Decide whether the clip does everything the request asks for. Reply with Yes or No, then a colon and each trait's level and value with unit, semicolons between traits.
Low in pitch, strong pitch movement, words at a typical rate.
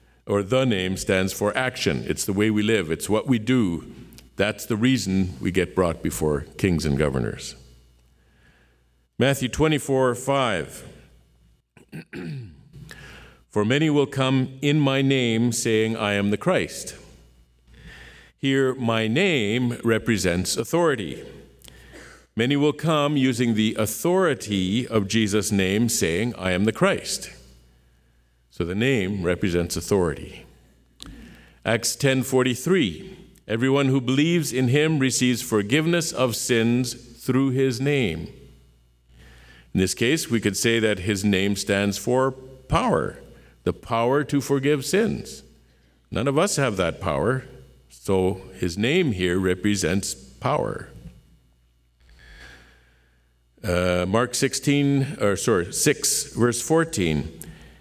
No: low, 110 Hz; wide, 8.4 semitones; slow, 120 wpm